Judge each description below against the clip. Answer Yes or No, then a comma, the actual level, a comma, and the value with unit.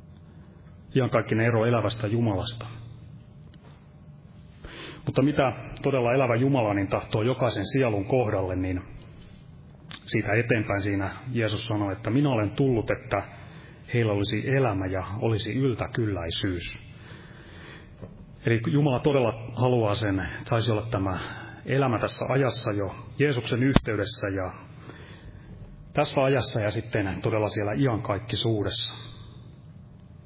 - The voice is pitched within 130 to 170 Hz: No, low, 115 Hz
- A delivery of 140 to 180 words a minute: No, average, 105 wpm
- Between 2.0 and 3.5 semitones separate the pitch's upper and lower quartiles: No, average, 4.2 semitones